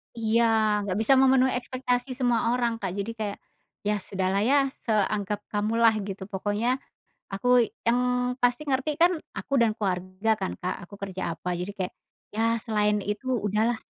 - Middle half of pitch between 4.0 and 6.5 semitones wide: No, average, 3.5 semitones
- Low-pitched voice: No, high, 220 Hz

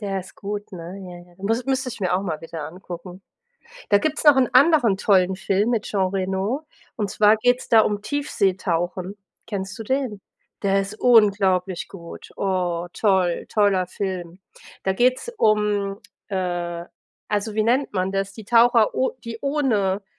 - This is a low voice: No, high, 200 Hz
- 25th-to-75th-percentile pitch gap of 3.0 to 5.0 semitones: Yes, average, 3.4 semitones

